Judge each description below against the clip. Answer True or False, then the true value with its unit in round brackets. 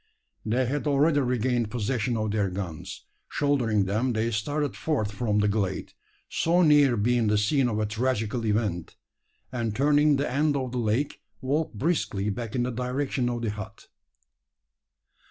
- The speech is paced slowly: False (160 wpm)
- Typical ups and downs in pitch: True (4.5 semitones)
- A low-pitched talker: True (120 Hz)